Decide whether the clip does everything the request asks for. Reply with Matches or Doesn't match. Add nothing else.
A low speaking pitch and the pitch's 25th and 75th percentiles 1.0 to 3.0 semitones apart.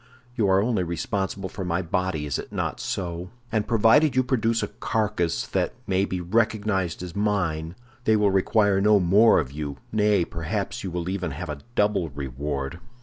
Doesn't match